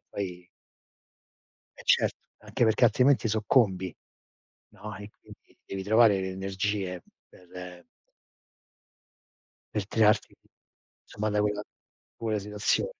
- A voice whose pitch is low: Yes, low, 105 Hz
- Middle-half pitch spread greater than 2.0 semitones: Yes, narrow, 2.4 semitones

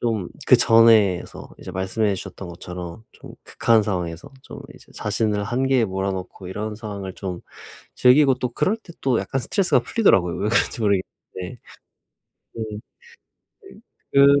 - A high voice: No, low, 105 Hz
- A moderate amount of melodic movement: Yes, average, 4.4 semitones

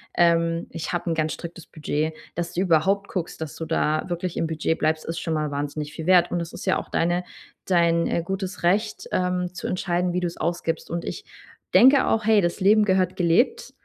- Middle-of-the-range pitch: Yes, medium, 175 Hz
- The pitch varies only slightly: Yes, narrow, 2.2 semitones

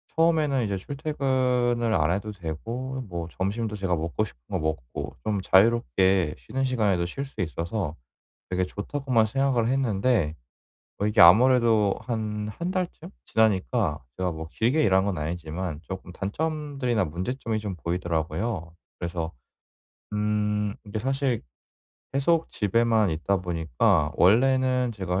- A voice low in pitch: Yes, low, 105 Hz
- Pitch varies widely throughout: Yes, wide, 6.0 semitones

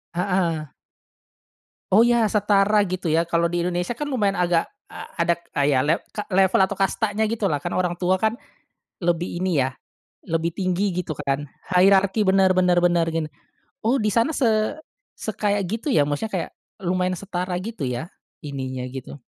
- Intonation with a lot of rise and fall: No, average, 3.5 semitones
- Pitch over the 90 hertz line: Yes, medium, 185 Hz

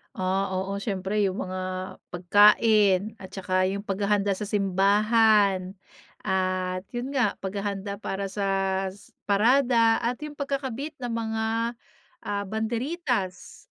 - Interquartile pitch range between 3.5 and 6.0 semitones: No, average, 3.0 semitones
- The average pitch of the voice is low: No, high, 205 Hz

